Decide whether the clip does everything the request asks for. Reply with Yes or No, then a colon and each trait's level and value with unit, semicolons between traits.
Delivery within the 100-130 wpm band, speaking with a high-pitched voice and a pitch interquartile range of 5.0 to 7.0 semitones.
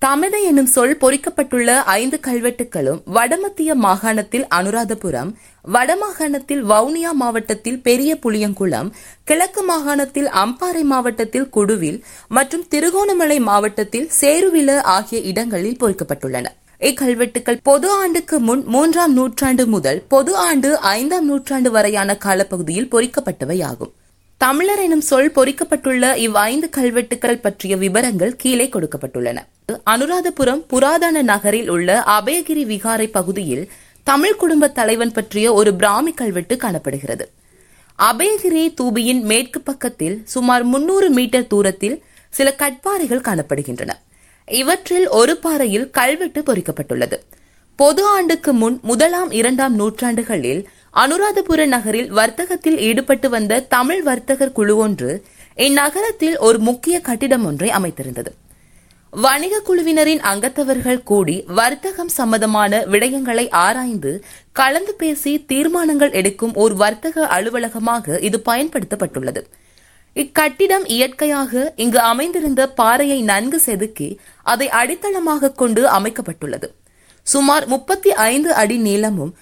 Yes: average, 105 wpm; very high, 250 Hz; wide, 5.6 semitones